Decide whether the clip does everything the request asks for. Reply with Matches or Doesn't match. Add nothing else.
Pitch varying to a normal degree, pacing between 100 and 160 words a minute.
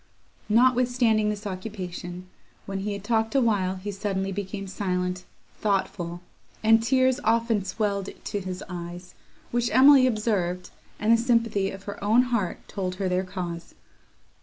Matches